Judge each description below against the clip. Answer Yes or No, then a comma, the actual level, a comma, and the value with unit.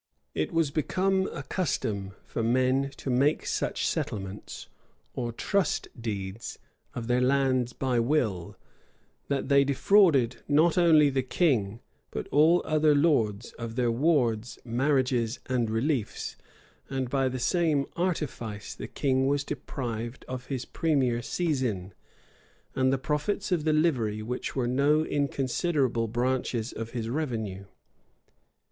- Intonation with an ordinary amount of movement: Yes, average, 4.2 semitones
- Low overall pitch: Yes, low, 130 Hz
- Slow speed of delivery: Yes, slow, 130 wpm